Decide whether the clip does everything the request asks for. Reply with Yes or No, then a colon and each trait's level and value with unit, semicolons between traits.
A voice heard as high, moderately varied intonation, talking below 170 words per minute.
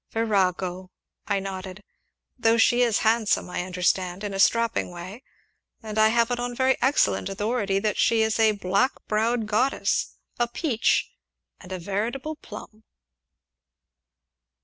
Yes: high, 215 Hz; average, 3.3 semitones; average, 140 wpm